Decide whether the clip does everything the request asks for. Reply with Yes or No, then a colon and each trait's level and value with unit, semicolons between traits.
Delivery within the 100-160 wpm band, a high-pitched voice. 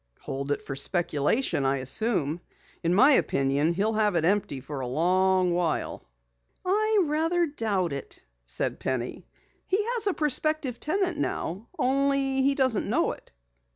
Yes: average, 150 wpm; high, 205 Hz